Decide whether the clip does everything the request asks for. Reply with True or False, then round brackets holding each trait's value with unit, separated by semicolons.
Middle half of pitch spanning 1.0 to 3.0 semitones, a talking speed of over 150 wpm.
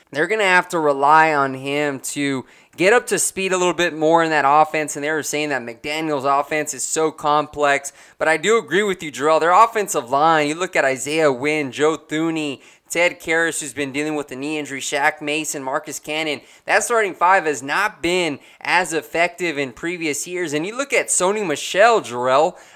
True (2.6 semitones; 205 wpm)